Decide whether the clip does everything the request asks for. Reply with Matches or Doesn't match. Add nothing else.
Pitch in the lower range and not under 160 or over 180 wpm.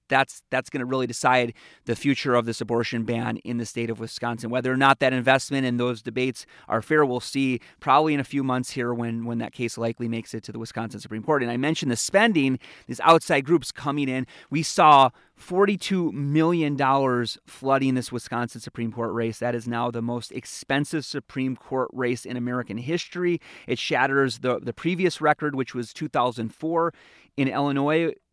Doesn't match